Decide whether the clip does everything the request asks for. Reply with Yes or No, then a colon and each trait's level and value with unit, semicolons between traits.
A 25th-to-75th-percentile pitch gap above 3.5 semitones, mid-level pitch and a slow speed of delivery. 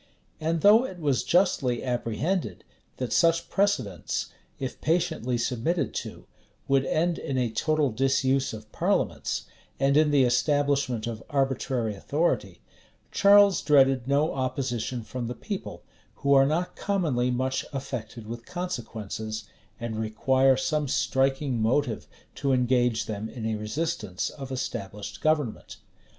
No: average, 4.4 semitones; low, 130 Hz; slow, 130 wpm